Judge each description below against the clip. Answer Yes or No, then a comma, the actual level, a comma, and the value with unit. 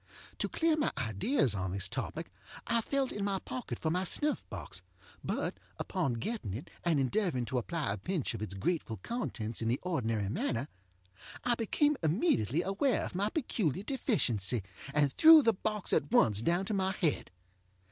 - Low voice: No, medium, 170 Hz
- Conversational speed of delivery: Yes, average, 175 wpm